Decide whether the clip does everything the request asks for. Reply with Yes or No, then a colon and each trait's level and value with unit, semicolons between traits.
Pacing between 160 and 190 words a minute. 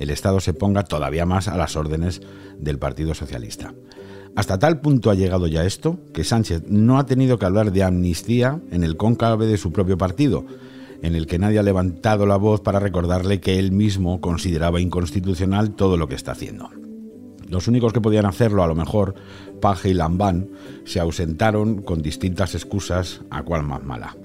Yes: average, 185 wpm